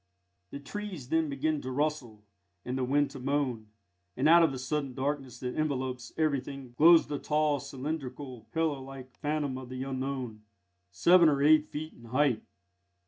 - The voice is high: No, medium, 140 Hz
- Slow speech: No, average, 165 wpm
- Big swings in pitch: No, average, 2.9 semitones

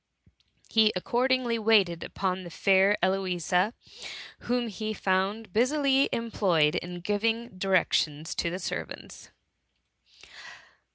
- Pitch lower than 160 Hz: No, high, 200 Hz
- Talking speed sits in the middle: No, slow, 105 wpm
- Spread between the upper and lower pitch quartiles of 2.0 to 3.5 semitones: No, average, 3.9 semitones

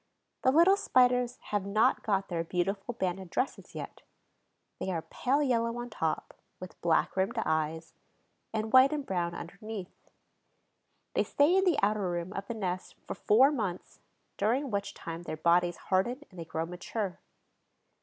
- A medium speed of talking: Yes, average, 160 wpm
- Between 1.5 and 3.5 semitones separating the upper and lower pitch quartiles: No, wide, 5.5 semitones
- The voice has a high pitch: Yes, high, 200 Hz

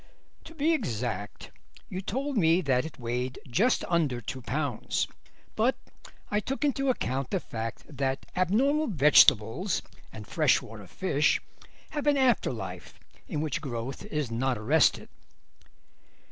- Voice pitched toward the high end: No, medium, 150 Hz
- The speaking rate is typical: No, slow, 130 wpm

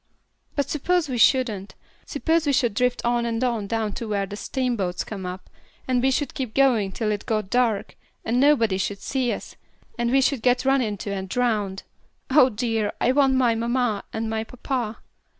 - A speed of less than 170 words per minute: No, average, 190 wpm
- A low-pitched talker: No, high, 235 Hz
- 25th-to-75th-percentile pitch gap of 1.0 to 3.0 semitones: No, average, 3.5 semitones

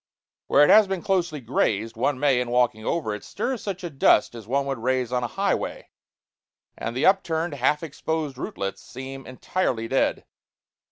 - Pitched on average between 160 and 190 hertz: No, low, 135 Hz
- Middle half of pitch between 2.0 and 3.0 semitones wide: No, average, 5.1 semitones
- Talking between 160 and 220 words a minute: Yes, average, 175 wpm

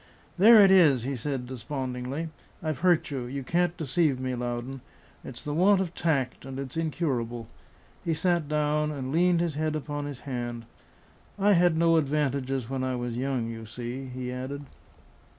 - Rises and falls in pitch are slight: No, average, 4.2 semitones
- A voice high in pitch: No, medium, 140 Hz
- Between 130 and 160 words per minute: No, average, 170 wpm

